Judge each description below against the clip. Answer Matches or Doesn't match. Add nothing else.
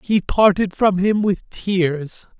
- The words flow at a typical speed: Matches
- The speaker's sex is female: Doesn't match